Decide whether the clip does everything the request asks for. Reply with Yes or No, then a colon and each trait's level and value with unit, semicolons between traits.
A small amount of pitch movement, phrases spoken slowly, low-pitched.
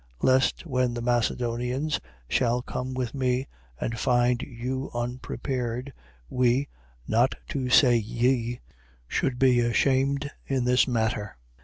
Yes: narrow, 1.6 semitones; slow, 120 wpm; low, 125 Hz